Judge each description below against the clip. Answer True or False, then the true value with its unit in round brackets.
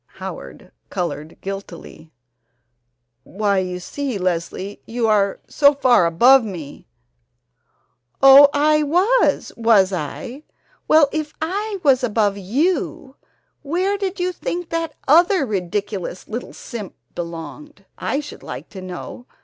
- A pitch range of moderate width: False (8.0 semitones)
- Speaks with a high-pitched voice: True (240 Hz)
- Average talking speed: False (125 wpm)